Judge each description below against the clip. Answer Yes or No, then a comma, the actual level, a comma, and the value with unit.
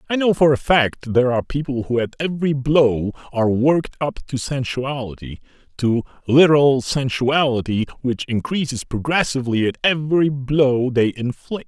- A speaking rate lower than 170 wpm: Yes, average, 145 wpm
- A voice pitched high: No, low, 135 Hz